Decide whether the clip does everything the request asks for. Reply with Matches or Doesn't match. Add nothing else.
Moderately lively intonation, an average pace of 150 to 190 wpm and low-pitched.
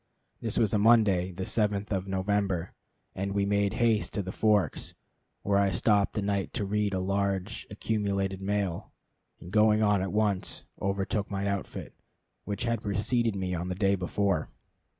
Doesn't match